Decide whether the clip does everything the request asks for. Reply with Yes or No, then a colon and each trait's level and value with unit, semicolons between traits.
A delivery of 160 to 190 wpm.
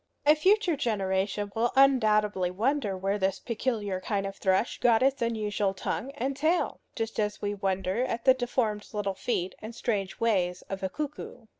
Yes: average, 170 wpm